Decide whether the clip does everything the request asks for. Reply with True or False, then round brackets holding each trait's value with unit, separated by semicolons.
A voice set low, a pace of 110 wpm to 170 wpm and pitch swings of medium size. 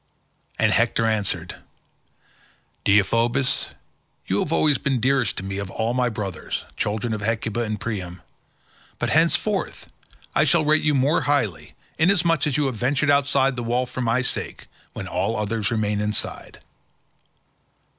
True (120 Hz; 155 wpm; 4.9 semitones)